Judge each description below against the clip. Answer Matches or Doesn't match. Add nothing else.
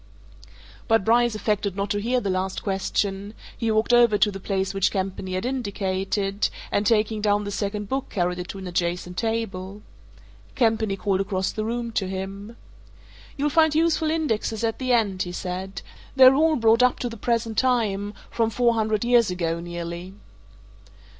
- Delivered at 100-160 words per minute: Doesn't match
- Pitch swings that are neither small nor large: Matches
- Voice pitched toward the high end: Matches